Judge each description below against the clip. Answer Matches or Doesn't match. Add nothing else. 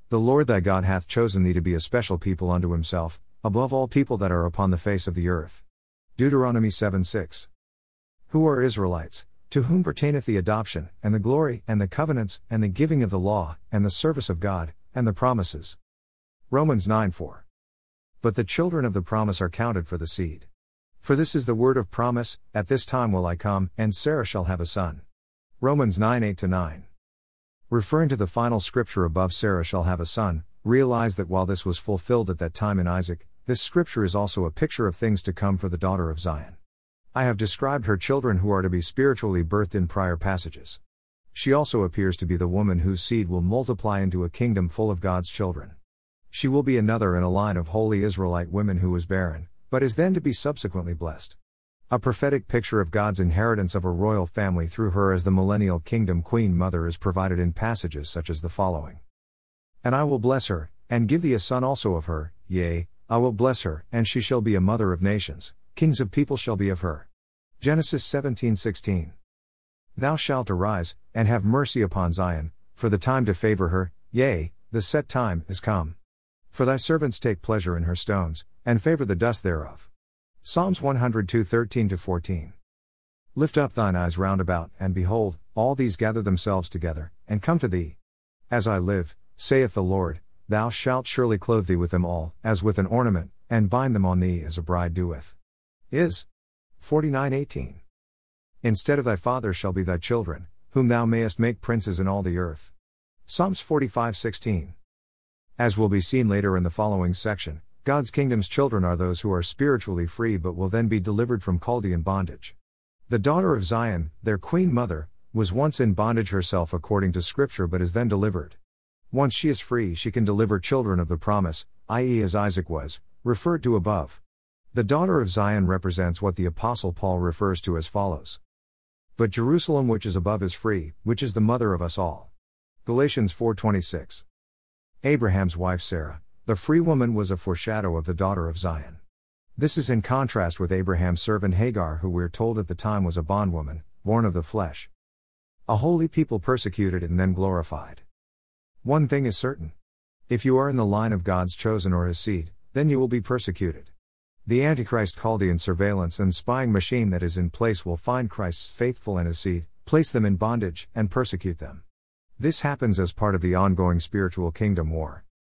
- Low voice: Matches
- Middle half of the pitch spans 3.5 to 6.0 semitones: Matches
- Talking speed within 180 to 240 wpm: Matches